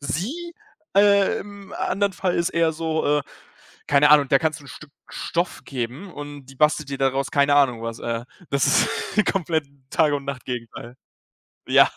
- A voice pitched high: No, medium, 145 Hz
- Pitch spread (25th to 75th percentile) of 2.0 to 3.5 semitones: No, average, 4.3 semitones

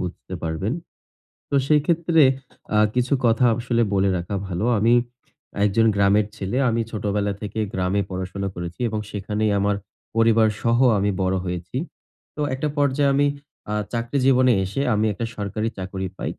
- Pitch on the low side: Yes, low, 105 Hz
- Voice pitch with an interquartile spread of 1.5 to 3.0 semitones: No, average, 3.6 semitones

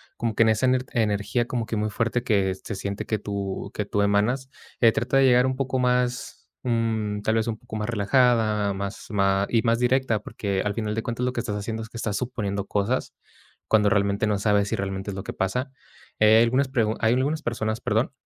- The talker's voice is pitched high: No, low, 110 Hz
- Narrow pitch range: No, average, 3.1 semitones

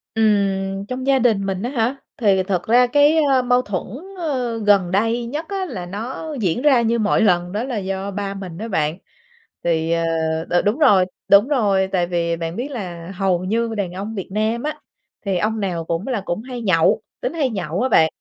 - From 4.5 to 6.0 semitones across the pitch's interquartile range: Yes, average, 4.8 semitones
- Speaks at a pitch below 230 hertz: Yes, high, 205 Hz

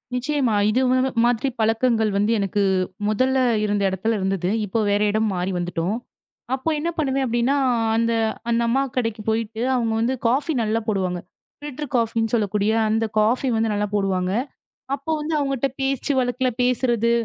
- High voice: Yes, high, 230 Hz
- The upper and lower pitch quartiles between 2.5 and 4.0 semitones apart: Yes, average, 3.5 semitones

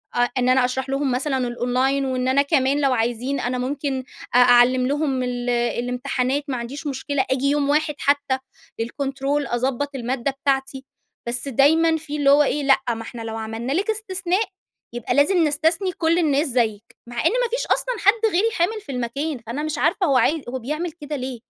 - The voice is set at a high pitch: Yes, very high, 275 Hz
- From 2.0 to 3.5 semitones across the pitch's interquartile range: Yes, average, 3.2 semitones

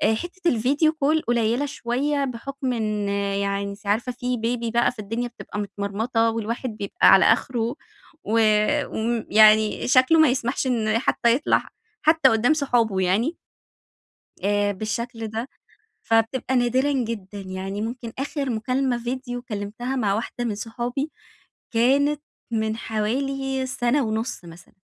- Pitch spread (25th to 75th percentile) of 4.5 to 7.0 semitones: No, average, 3.3 semitones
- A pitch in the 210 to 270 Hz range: Yes, high, 235 Hz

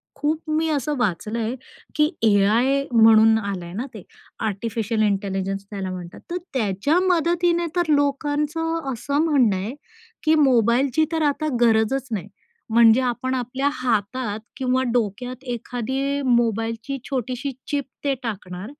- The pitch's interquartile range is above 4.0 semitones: Yes, average, 4.6 semitones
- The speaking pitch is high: Yes, high, 245 Hz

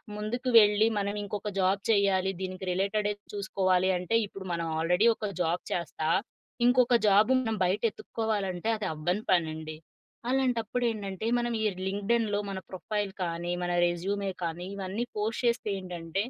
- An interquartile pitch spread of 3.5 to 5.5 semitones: No, average, 3.0 semitones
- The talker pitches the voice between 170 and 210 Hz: Yes, high, 195 Hz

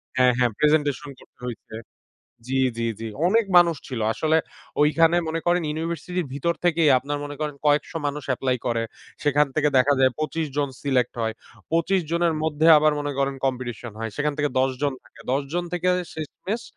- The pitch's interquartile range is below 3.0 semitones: No, average, 3.6 semitones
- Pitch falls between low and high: Yes, medium, 150 Hz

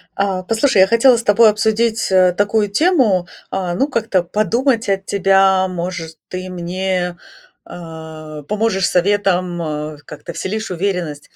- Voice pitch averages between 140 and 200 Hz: Yes, high, 190 Hz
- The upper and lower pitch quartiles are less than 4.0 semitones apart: Yes, average, 3.4 semitones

